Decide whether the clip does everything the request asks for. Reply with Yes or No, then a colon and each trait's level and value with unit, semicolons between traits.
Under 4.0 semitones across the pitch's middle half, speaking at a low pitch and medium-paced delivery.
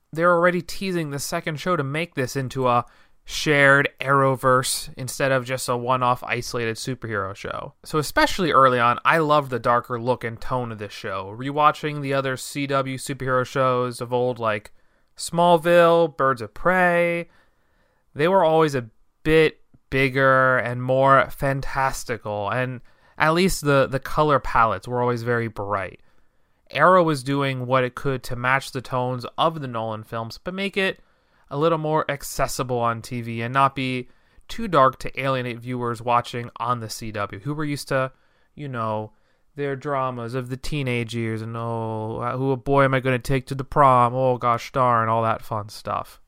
Yes: average, 2.9 semitones; low, 130 Hz; average, 175 wpm